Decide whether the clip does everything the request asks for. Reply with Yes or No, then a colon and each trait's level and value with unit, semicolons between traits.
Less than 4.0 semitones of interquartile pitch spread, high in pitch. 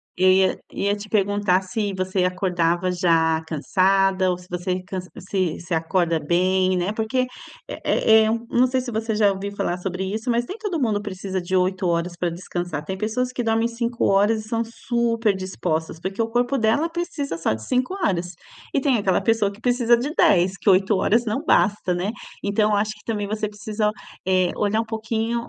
Yes: average, 3.6 semitones; high, 200 Hz